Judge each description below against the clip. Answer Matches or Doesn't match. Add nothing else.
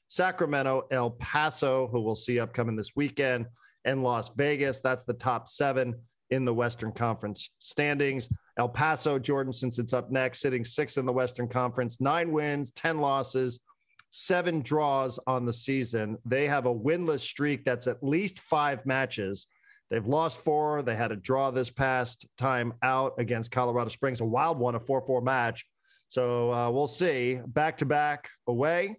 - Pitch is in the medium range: Doesn't match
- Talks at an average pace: Matches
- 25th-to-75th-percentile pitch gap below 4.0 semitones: Matches